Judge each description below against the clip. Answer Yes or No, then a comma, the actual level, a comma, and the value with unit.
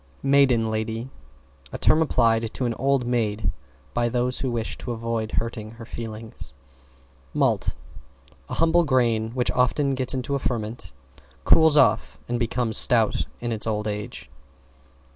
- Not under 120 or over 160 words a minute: Yes, average, 145 wpm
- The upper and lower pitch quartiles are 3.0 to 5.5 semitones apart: No, narrow, 2.5 semitones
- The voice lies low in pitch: Yes, low, 120 Hz